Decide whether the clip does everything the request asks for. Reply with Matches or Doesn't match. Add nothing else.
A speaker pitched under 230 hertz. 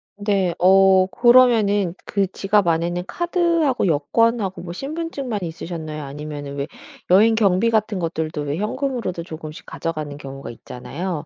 Matches